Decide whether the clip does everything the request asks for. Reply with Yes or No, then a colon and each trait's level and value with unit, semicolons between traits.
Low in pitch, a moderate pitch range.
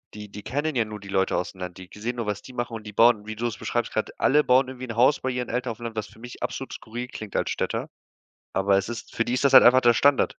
Yes: low, 115 Hz; average, 3.1 semitones